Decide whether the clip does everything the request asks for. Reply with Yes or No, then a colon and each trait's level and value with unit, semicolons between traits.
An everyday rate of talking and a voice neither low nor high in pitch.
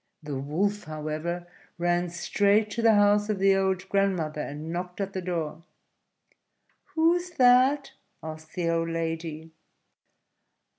No: slow, 130 wpm; medium, 175 Hz